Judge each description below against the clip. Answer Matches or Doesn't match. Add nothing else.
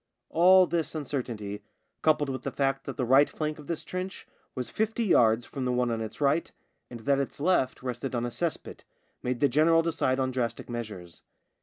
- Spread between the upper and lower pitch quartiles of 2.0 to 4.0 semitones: Doesn't match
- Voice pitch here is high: Doesn't match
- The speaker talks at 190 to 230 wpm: Matches